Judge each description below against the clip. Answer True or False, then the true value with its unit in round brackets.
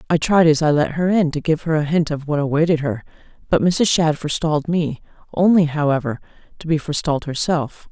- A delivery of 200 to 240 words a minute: True (205 wpm)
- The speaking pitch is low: False (155 Hz)